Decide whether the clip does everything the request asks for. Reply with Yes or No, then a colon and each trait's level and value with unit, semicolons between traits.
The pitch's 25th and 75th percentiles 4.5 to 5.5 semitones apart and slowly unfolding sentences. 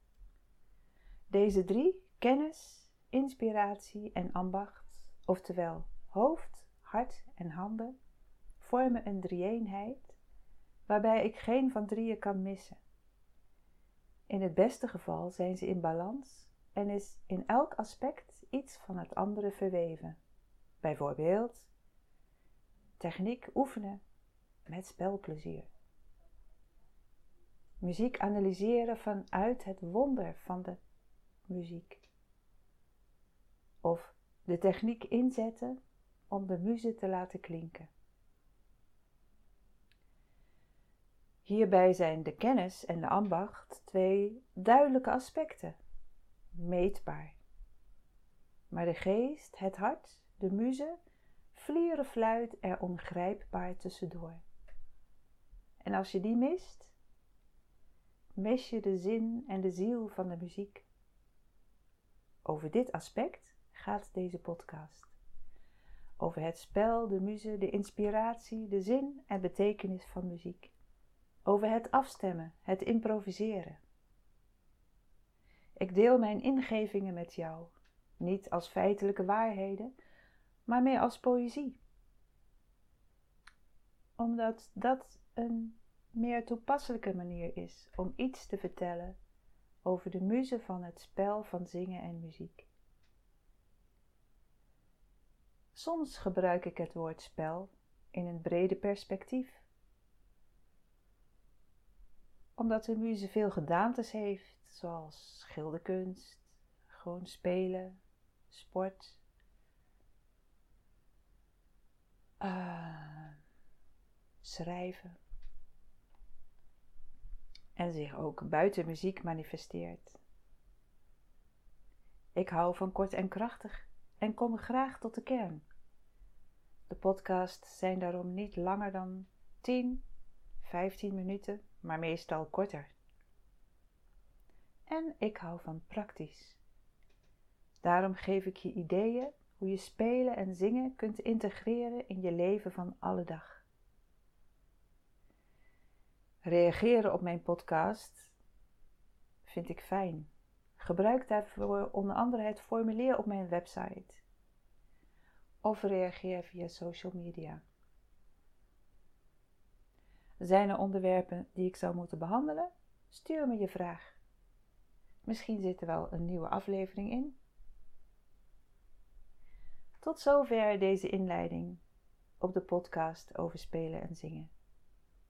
Yes: average, 4.9 semitones; slow, 100 wpm